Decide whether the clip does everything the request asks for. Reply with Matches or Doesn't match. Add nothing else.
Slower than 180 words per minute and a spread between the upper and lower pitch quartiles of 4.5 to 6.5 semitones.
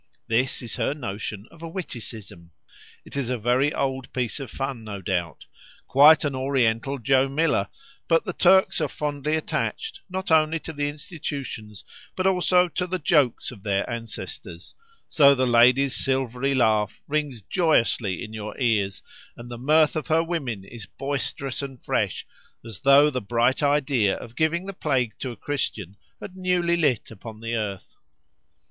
Matches